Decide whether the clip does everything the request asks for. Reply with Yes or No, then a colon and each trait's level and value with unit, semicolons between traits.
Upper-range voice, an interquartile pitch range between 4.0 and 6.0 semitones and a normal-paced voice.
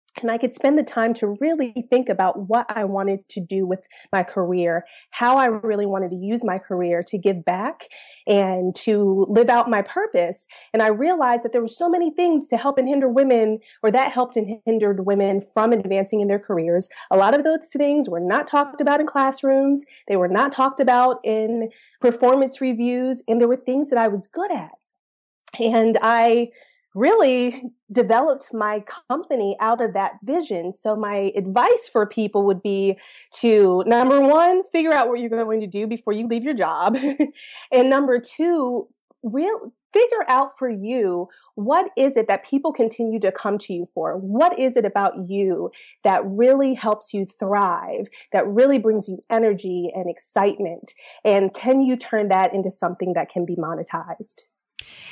Yes: high, 230 Hz; average, 5.1 semitones; average, 180 wpm